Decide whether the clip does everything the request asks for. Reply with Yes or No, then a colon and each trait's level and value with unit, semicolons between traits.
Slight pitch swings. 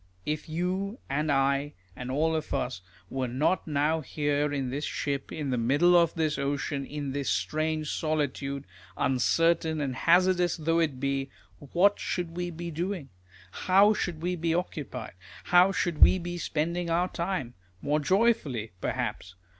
No: average, 3.9 semitones